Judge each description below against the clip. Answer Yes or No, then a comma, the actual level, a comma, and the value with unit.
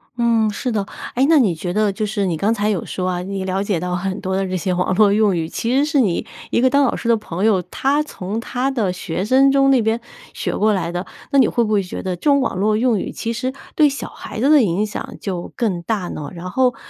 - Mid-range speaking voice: No, high, 210 Hz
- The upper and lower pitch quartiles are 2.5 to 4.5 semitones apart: No, average, 4.9 semitones